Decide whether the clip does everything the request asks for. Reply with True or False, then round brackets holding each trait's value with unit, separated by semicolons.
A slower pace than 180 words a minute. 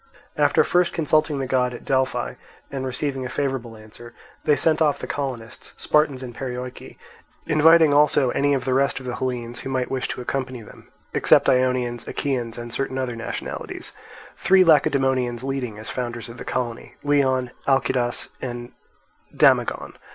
True (160 wpm)